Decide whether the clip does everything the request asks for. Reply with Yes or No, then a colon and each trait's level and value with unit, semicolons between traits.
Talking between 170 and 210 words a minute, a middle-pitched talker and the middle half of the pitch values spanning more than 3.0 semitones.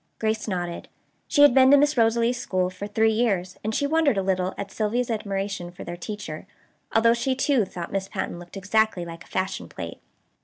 No: average, 200 wpm; high, 205 Hz; average, 4.2 semitones